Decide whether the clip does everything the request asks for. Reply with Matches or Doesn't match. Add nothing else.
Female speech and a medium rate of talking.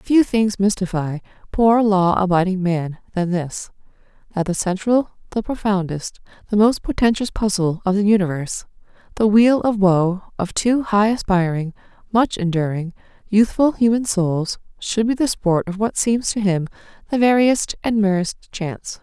Matches